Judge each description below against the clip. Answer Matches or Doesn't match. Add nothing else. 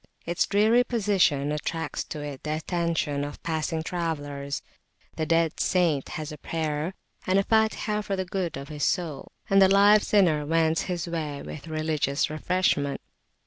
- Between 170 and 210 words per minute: Doesn't match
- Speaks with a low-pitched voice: Doesn't match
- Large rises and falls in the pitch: Doesn't match